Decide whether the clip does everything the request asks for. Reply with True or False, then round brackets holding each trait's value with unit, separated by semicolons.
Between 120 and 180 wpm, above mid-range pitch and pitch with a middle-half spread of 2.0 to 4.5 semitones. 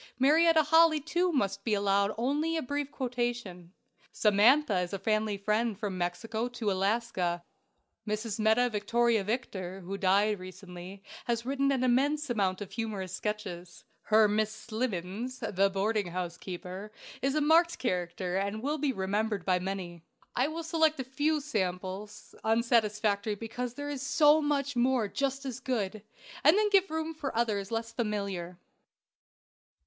False (150 wpm; 220 Hz; 5.3 semitones)